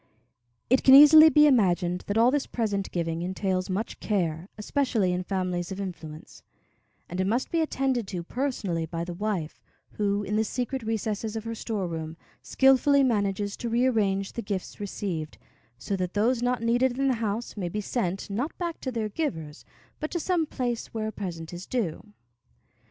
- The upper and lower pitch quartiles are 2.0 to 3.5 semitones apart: No, average, 5.2 semitones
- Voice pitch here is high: Yes, high, 210 Hz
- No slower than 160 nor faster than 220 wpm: Yes, average, 180 wpm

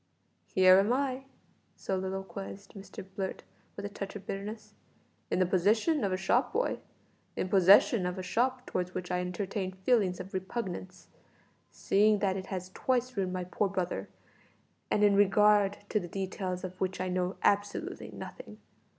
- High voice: Yes, high, 195 Hz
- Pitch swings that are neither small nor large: No, narrow, 2.1 semitones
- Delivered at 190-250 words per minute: No, average, 160 wpm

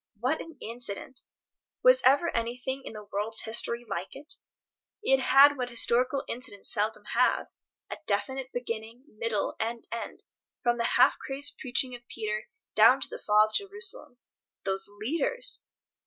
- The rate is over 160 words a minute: No, average, 150 wpm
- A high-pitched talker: Yes, high, 240 Hz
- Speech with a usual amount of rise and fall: Yes, average, 3.7 semitones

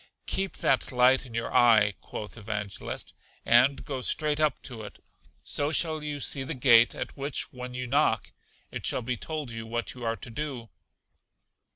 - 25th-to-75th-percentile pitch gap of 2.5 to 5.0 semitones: Yes, average, 3.8 semitones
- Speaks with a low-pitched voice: Yes, low, 125 Hz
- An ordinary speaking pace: Yes, average, 180 wpm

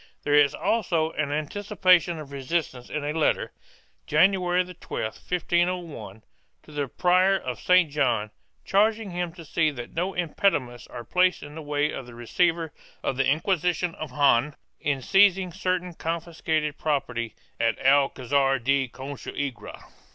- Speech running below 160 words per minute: Yes, average, 145 wpm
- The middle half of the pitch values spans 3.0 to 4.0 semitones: No, average, 4.6 semitones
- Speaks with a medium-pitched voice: Yes, medium, 155 Hz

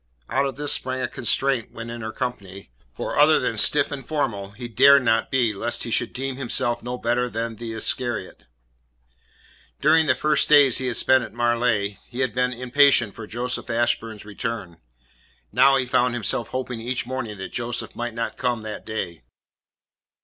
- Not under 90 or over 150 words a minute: No, average, 180 wpm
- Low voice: Yes, low, 120 Hz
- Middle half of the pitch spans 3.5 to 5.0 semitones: No, narrow, 2.5 semitones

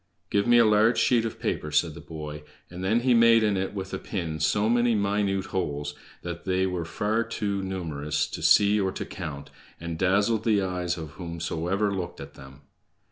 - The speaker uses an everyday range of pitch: Yes, average, 4.1 semitones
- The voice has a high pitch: No, very low, 95 Hz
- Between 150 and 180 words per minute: No, average, 195 wpm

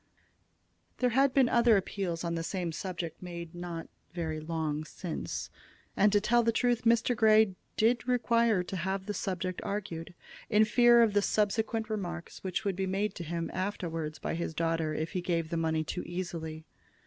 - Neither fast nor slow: Yes, average, 180 wpm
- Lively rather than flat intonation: No, average, 4.7 semitones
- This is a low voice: No, medium, 185 Hz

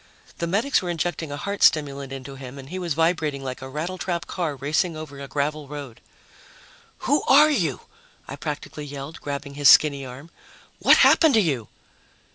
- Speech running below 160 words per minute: No, average, 175 wpm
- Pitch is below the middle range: No, medium, 150 Hz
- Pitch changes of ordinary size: Yes, average, 3.6 semitones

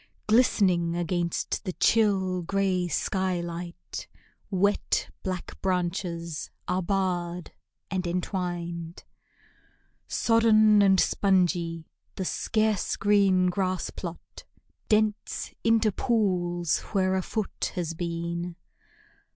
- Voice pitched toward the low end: No, medium, 185 Hz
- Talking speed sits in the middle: No, slow, 95 wpm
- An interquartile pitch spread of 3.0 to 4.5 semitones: No, narrow, 2.5 semitones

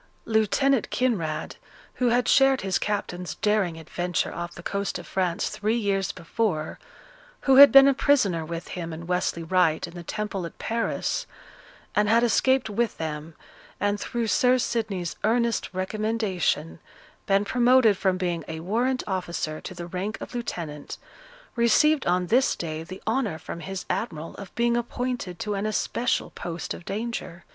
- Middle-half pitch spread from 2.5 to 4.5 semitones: No, wide, 5.4 semitones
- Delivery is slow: No, average, 160 wpm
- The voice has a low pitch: No, high, 200 Hz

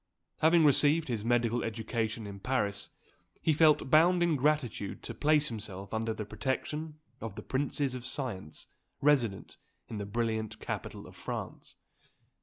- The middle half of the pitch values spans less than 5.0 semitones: No, average, 5.3 semitones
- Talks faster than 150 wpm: No, average, 145 wpm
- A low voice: Yes, low, 120 Hz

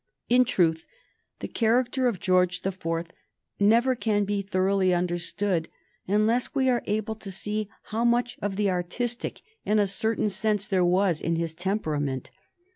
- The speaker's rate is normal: Yes, average, 155 wpm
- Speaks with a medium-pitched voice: No, high, 200 Hz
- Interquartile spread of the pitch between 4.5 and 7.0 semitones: No, average, 3.7 semitones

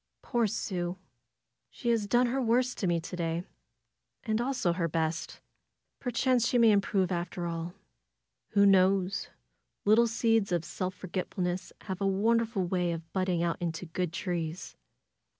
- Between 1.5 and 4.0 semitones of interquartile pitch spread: No, average, 4.4 semitones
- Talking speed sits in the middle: Yes, average, 150 wpm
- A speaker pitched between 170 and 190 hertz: Yes, medium, 185 Hz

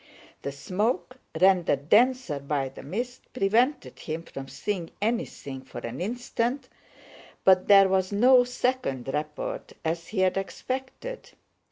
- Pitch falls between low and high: No, high, 195 Hz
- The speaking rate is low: Yes, slow, 130 wpm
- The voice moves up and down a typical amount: No, wide, 8.5 semitones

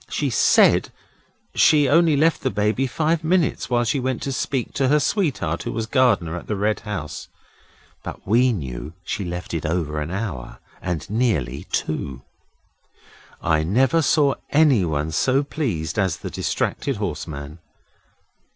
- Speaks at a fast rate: No, average, 150 wpm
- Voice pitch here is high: No, low, 105 Hz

